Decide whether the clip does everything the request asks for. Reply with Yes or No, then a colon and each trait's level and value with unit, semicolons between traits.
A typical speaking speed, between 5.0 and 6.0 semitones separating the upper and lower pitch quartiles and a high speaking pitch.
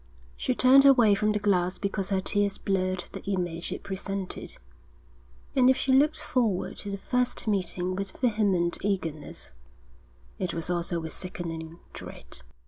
No: average, 150 wpm; average, 3.4 semitones; high, 195 Hz